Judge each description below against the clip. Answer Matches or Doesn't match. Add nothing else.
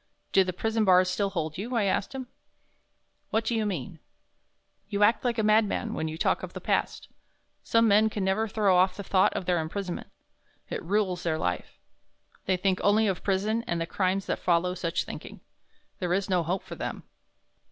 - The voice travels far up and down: Doesn't match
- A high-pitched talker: Matches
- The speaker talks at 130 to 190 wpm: Doesn't match